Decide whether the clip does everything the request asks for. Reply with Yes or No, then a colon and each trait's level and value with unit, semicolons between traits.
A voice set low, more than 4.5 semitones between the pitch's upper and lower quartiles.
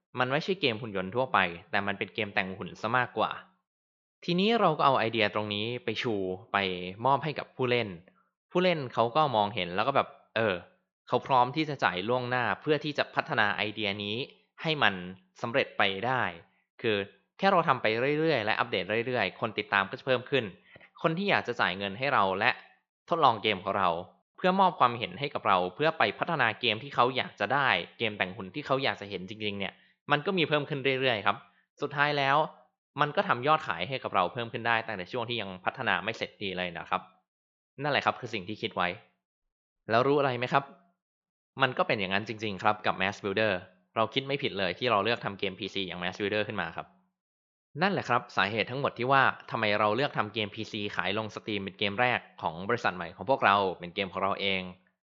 Yes: low, 110 Hz; wide, 5.6 semitones